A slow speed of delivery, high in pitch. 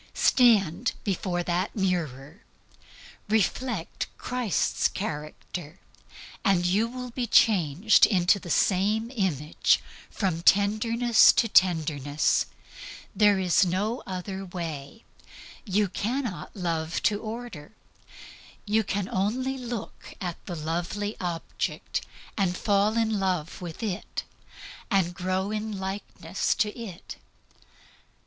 Yes: slow, 105 wpm; high, 195 Hz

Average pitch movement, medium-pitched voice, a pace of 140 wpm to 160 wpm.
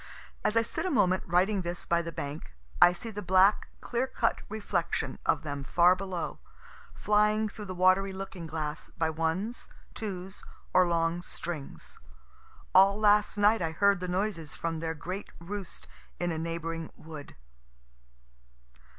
Yes: average, 3.7 semitones; medium, 180 Hz; average, 150 wpm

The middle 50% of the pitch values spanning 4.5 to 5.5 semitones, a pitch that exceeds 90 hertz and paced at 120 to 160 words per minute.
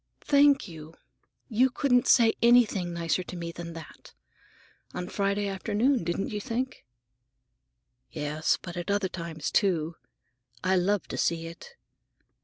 Yes: average, 5.2 semitones; high, 190 Hz; slow, 135 wpm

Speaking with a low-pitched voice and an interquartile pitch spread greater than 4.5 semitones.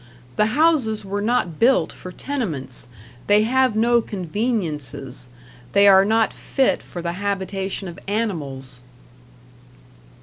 No: high, 200 Hz; average, 4.9 semitones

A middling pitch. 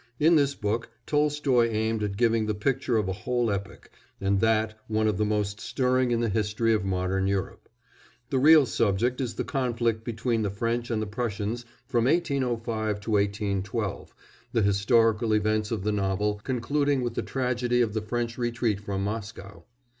No: low, 110 Hz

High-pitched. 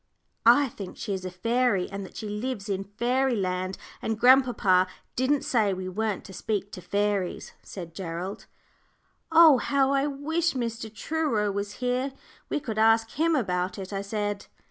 Yes: high, 215 Hz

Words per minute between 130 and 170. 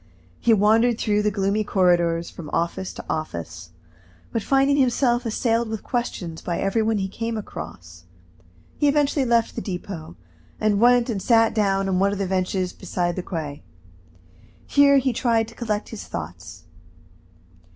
Yes: average, 160 wpm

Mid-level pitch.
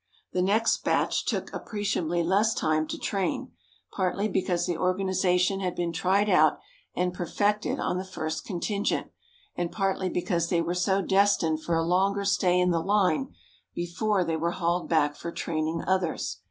Yes: medium, 180 Hz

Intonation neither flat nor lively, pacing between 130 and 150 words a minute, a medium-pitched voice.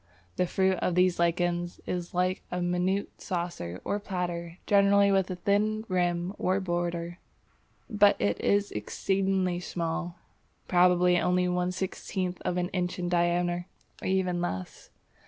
No: narrow, 1.5 semitones; average, 140 wpm; medium, 180 Hz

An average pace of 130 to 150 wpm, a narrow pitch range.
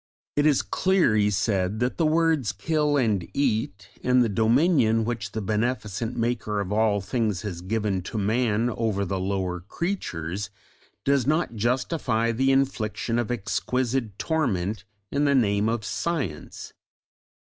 No: average, 145 wpm; average, 4.3 semitones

